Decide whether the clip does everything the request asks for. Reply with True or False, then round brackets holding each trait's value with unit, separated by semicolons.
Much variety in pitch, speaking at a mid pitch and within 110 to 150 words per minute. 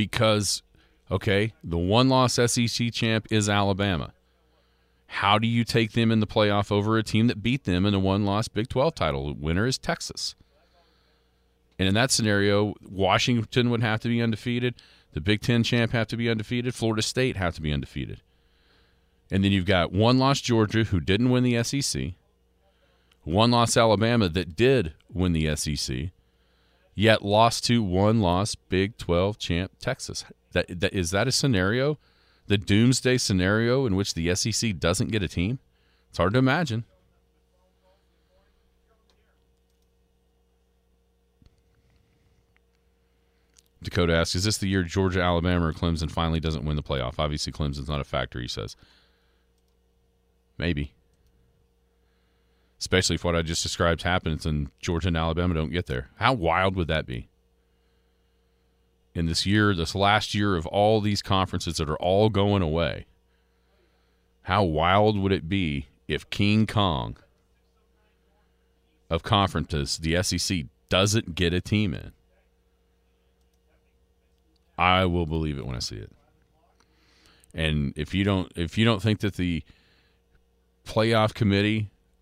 False (5.7 semitones; 95 Hz; 145 wpm)